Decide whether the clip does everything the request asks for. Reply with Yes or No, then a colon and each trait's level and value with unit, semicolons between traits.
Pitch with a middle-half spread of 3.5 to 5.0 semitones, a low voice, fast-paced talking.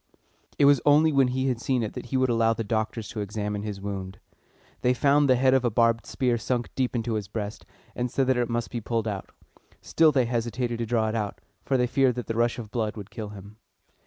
No: average, 2.8 semitones; low, 120 Hz; fast, 245 wpm